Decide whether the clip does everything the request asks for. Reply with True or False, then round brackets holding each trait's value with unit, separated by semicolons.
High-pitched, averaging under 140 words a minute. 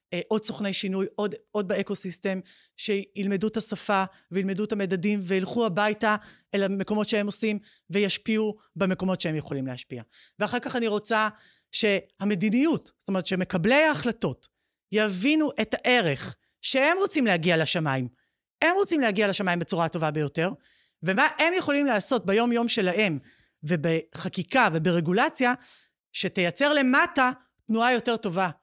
True (205 Hz; 130 wpm)